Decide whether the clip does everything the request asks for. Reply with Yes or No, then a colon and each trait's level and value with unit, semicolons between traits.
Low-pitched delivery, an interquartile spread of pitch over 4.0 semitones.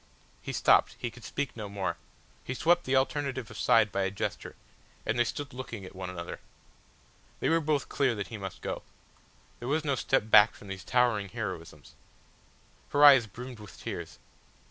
Yes: low, 115 Hz; average, 4.9 semitones